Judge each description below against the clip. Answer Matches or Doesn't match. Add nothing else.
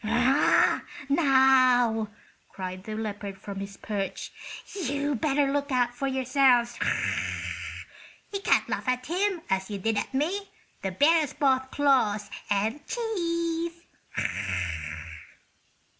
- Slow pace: Matches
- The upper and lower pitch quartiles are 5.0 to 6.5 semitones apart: Matches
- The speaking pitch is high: Matches